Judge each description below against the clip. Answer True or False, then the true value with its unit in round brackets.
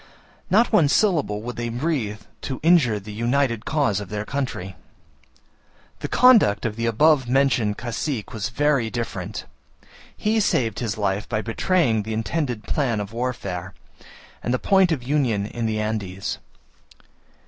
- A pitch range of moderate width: True (5.0 semitones)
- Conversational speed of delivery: True (150 wpm)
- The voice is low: True (120 Hz)